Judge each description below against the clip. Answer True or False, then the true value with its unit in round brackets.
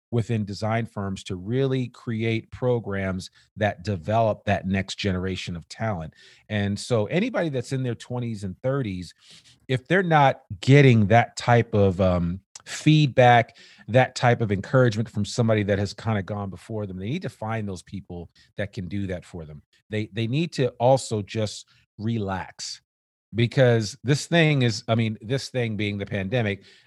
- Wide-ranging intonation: False (3.9 semitones)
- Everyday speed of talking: True (170 wpm)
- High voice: False (110 Hz)